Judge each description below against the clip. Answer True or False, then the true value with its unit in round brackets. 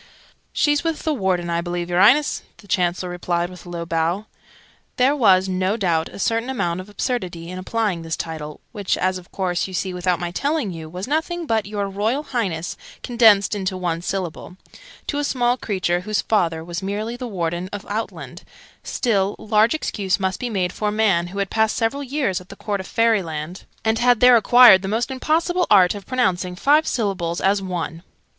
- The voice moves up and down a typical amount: True (4.6 semitones)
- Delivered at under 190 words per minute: False (195 wpm)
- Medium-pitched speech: False (195 Hz)